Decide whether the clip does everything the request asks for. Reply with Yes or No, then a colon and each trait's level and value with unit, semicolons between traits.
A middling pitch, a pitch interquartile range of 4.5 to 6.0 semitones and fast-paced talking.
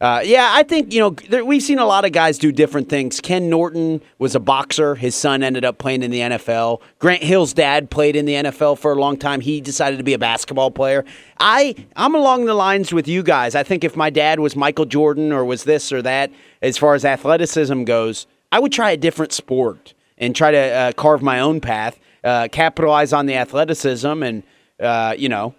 No: medium, 150 Hz; average, 3.6 semitones; fast, 225 wpm